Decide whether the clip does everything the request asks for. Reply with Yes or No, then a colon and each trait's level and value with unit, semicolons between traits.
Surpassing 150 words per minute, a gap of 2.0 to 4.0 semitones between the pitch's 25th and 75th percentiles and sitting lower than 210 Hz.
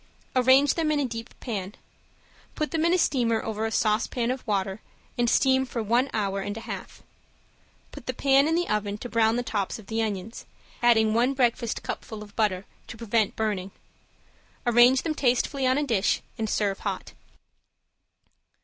No: average, 175 wpm; average, 3.5 semitones; high, 230 Hz